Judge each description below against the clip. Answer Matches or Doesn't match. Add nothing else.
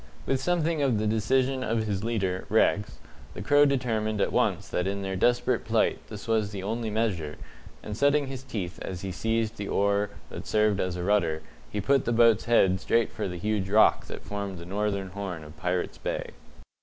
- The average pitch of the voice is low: Matches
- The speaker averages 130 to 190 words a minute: Doesn't match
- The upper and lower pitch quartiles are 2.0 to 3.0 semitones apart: Doesn't match